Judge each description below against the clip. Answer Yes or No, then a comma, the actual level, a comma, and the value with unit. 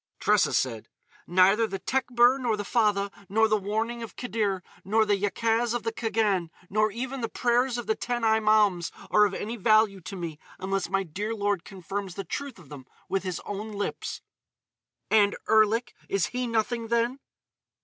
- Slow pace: No, average, 175 wpm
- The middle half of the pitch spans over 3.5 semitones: No, average, 2.9 semitones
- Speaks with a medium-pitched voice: No, high, 215 Hz